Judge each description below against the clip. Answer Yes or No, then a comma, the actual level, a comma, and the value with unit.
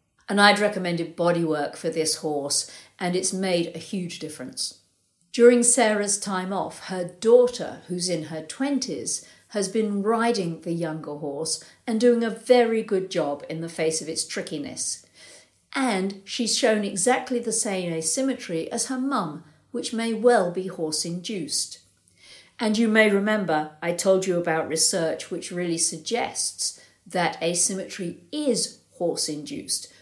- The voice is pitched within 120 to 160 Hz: No, medium, 185 Hz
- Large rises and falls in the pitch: Yes, wide, 5.7 semitones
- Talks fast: No, average, 150 wpm